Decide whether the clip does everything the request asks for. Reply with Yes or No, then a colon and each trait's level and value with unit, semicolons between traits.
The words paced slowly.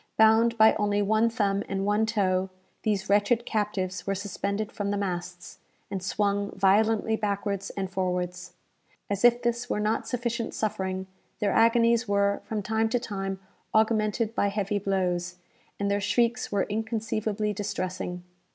No: average, 150 wpm